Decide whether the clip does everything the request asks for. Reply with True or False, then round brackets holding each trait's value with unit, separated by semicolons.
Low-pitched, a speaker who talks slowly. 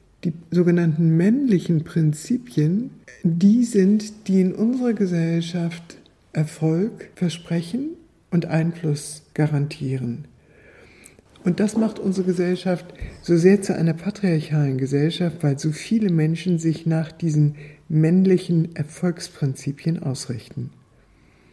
False (170 Hz; 100 wpm)